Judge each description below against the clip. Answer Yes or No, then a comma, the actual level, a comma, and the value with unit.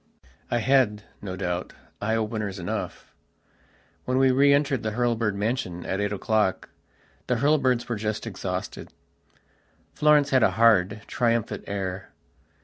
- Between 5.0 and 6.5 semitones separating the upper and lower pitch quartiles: No, average, 4.2 semitones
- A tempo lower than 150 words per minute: Yes, slow, 135 wpm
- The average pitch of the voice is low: Yes, low, 110 Hz